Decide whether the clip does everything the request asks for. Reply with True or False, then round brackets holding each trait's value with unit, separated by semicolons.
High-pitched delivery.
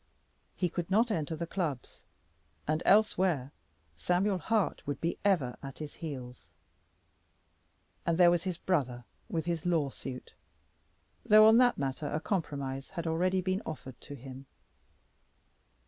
False (165 Hz)